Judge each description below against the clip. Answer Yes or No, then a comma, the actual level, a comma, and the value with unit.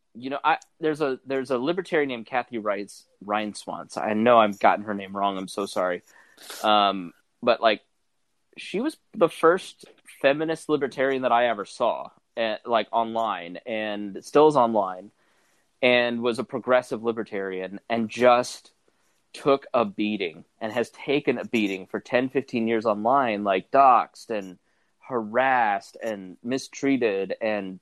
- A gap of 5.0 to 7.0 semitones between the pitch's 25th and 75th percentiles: No, average, 4.4 semitones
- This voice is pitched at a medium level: No, low, 115 Hz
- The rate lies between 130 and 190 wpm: Yes, average, 150 wpm